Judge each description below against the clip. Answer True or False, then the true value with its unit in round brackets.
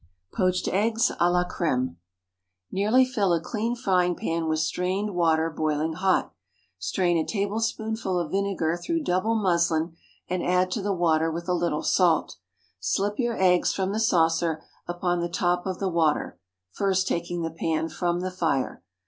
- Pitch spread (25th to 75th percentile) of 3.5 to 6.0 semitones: False (3.0 semitones)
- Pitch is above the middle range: False (180 Hz)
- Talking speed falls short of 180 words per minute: True (165 wpm)